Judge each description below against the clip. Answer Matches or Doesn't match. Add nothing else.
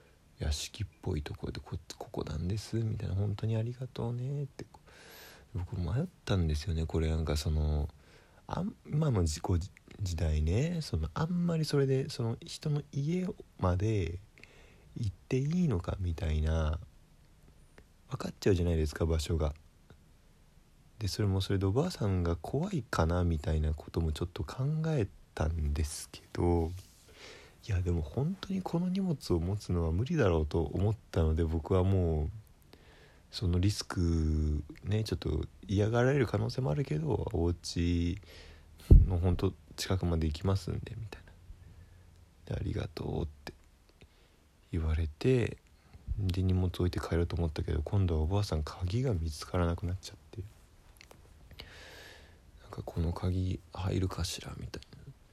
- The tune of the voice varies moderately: Matches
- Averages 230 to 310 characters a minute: Matches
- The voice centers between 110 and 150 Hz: Doesn't match